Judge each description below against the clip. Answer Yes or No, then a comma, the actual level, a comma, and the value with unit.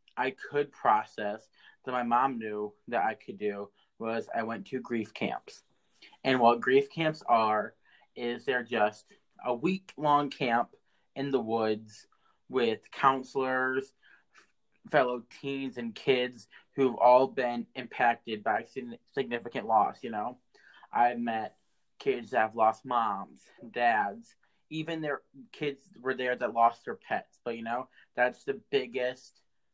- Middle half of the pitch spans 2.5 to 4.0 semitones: Yes, average, 2.9 semitones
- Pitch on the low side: Yes, low, 125 Hz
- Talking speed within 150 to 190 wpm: No, average, 140 wpm